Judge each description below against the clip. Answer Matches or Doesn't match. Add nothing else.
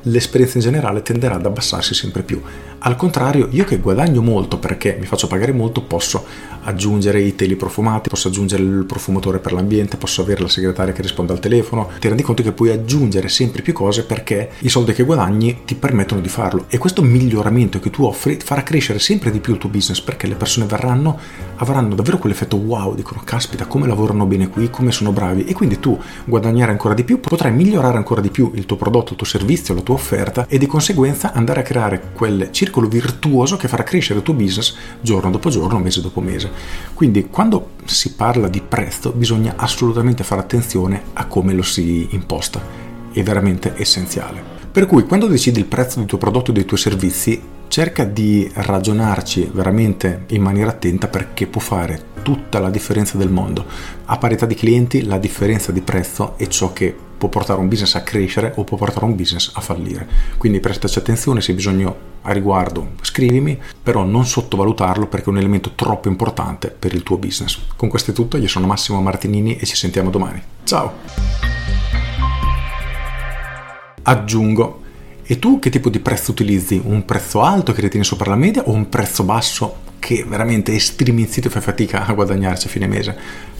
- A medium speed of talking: Doesn't match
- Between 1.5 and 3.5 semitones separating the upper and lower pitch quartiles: Doesn't match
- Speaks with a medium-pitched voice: Doesn't match